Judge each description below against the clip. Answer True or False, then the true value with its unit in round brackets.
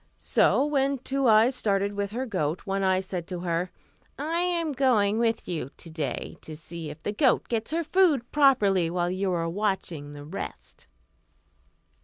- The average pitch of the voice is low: False (200 Hz)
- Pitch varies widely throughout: True (7.3 semitones)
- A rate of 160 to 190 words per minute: True (175 wpm)